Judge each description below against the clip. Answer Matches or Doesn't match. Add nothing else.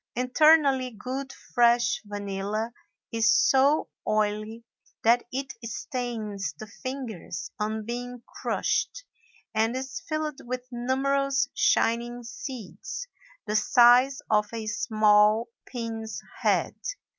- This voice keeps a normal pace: Doesn't match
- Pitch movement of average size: Matches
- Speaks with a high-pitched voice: Matches